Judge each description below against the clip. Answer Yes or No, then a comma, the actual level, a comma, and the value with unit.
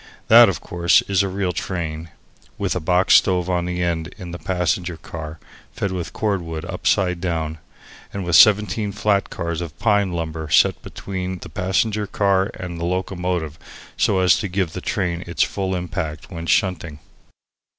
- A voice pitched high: No, very low, 90 Hz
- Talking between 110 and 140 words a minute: No, average, 165 wpm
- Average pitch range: No, narrow, 2.2 semitones